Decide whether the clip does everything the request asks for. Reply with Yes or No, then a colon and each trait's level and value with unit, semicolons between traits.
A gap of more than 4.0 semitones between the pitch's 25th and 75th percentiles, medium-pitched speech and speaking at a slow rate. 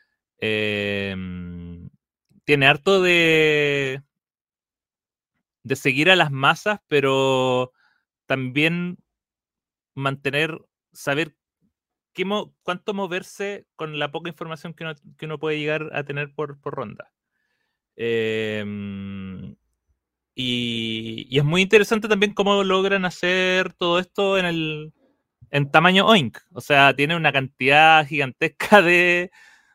Yes: wide, 5.5 semitones; medium, 155 Hz; slow, 115 wpm